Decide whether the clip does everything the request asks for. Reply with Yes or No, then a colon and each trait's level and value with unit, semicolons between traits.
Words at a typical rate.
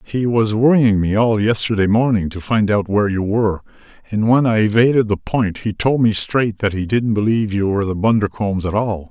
No: fast, 215 wpm